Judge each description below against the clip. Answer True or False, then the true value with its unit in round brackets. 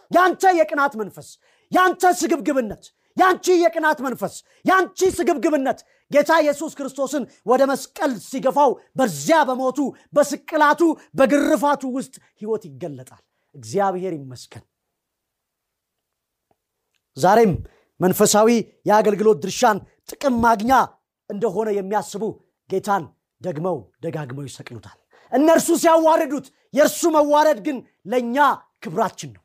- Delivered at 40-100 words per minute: True (90 wpm)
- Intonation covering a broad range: True (7.5 semitones)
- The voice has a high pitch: True (260 Hz)